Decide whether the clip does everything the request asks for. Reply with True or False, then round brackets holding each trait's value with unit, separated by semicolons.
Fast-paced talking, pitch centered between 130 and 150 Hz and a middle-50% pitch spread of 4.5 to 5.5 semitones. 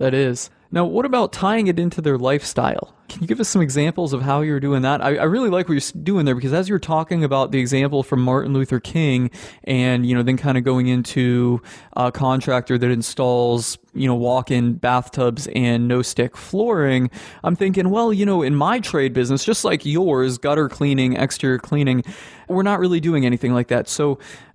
True (220 wpm; 135 Hz; 5.1 semitones)